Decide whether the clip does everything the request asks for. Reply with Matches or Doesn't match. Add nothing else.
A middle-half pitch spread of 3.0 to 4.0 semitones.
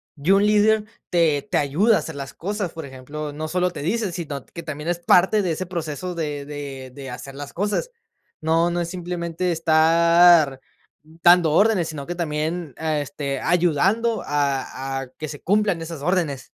Matches